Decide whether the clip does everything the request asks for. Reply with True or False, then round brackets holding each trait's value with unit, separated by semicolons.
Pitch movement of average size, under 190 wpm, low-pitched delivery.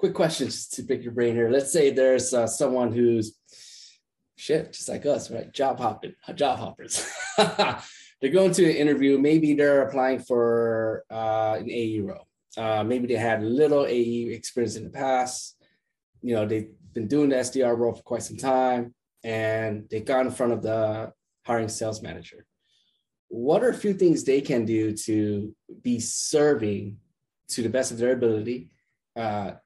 True (3.1 semitones; 170 wpm; 120 Hz)